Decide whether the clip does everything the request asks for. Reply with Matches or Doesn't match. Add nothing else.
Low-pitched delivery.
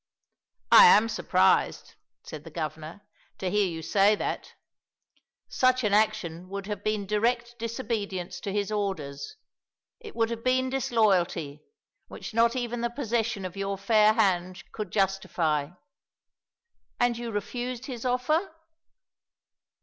Doesn't match